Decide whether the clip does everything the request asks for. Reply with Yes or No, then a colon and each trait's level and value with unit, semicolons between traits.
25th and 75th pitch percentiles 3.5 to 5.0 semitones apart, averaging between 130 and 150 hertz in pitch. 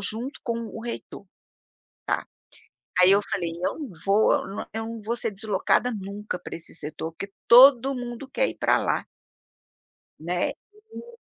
No: average, 3.9 semitones; high, 220 Hz